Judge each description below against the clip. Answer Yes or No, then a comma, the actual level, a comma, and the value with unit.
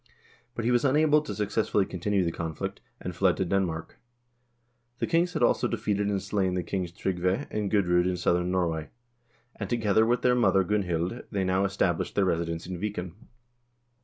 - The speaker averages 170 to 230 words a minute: Yes, average, 180 wpm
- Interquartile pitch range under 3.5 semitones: Yes, average, 3.1 semitones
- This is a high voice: No, very low, 95 Hz